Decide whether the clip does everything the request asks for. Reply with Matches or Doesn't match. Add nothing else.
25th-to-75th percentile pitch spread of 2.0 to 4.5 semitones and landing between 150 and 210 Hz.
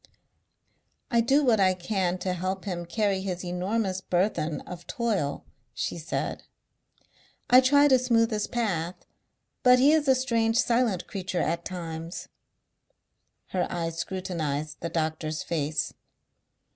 Doesn't match